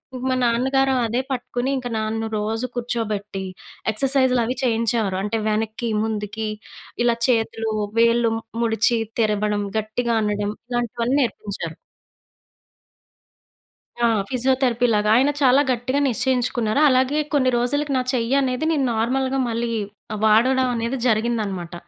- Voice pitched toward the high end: Yes, high, 235 Hz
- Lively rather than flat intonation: No, average, 2.8 semitones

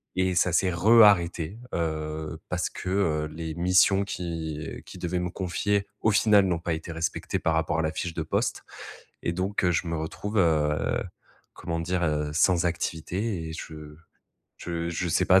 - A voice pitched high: No, very low, 85 Hz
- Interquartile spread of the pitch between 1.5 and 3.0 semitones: Yes, narrow, 2.5 semitones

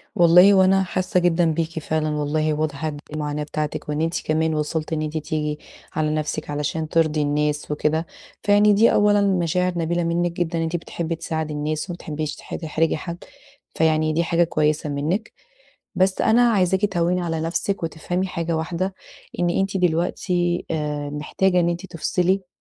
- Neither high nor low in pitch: Yes, medium, 165 Hz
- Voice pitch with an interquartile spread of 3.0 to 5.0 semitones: No, narrow, 2.6 semitones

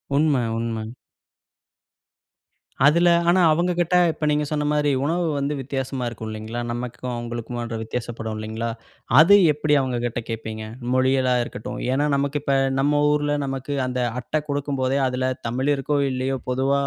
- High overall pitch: No, low, 130 Hz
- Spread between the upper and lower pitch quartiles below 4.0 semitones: Yes, average, 3.6 semitones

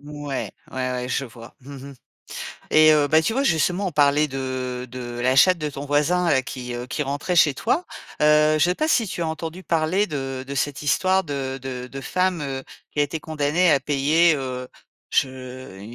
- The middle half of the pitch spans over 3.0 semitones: Yes, average, 3.5 semitones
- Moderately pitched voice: Yes, medium, 145 Hz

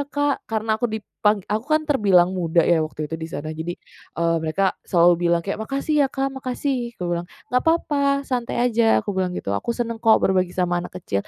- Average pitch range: No, wide, 6.4 semitones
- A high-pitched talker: Yes, high, 210 Hz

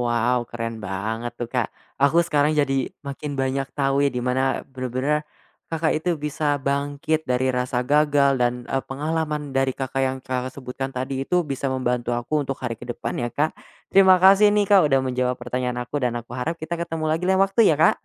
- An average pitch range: Yes, average, 3.5 semitones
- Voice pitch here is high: No, low, 135 Hz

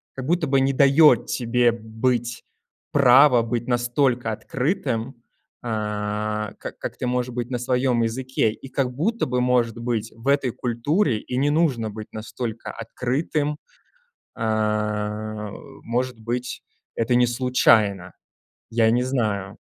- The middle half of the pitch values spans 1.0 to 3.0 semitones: Yes, average, 2.7 semitones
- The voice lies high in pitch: No, low, 120 Hz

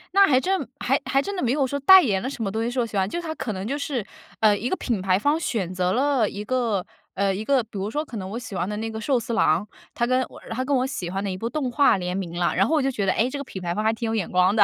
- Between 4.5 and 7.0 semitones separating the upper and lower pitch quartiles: Yes, wide, 5.4 semitones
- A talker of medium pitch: No, high, 225 Hz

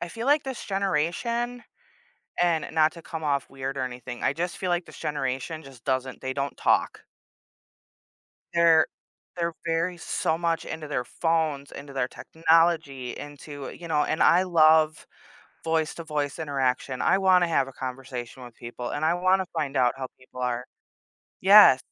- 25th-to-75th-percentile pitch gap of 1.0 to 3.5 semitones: No, average, 4.1 semitones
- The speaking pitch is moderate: Yes, medium, 155 Hz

